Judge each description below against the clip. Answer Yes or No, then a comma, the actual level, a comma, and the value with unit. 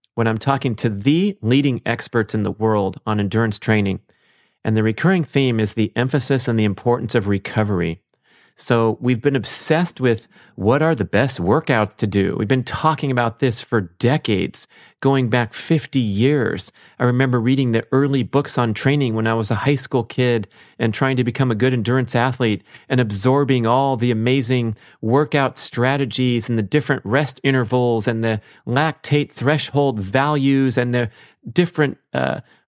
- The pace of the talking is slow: No, average, 170 wpm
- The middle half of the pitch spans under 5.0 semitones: Yes, average, 3.3 semitones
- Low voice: Yes, low, 125 Hz